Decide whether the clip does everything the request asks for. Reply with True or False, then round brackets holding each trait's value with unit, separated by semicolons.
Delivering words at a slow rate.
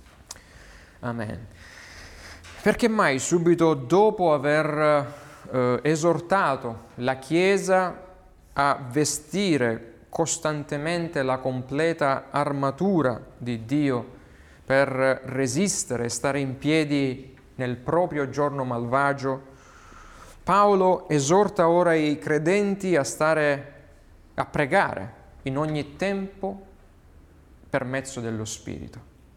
True (90 wpm)